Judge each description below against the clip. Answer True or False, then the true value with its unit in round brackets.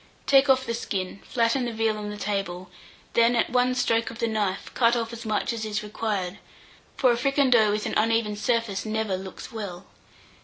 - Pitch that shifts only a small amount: True (2.2 semitones)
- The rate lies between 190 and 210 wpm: True (195 wpm)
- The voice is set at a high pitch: True (225 Hz)